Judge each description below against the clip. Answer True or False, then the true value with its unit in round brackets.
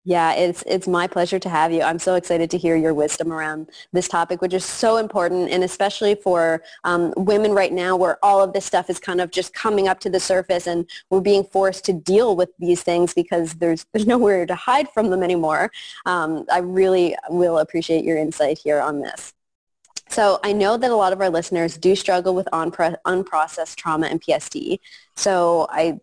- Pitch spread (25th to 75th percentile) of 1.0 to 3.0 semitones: True (2.6 semitones)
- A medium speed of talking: False (210 wpm)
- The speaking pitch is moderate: True (180 Hz)